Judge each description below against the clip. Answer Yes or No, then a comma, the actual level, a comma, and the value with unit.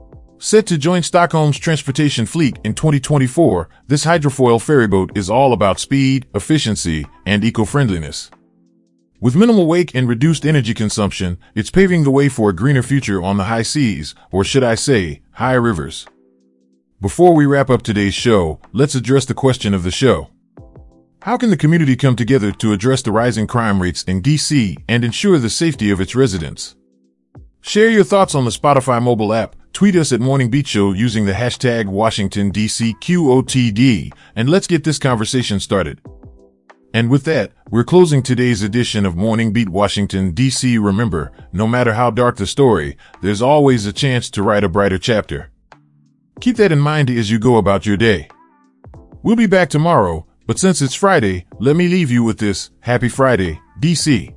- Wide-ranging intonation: Yes, wide, 6.2 semitones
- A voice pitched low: Yes, low, 120 Hz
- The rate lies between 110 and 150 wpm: No, average, 170 wpm